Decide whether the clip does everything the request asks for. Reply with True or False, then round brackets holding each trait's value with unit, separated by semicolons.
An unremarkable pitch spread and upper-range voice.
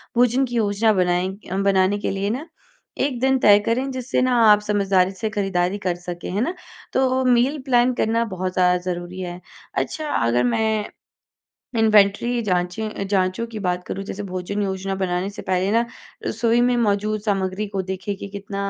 True (3.7 semitones; 200 Hz)